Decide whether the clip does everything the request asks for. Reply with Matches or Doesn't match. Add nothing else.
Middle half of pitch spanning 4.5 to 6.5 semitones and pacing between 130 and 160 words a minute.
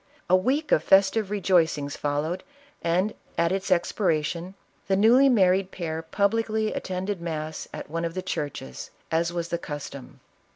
Doesn't match